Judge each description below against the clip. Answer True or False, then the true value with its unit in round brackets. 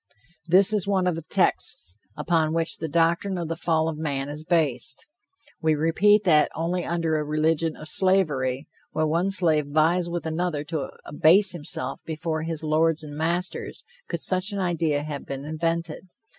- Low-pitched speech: False (160 Hz)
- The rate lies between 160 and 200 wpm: True (170 wpm)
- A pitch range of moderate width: False (2.2 semitones)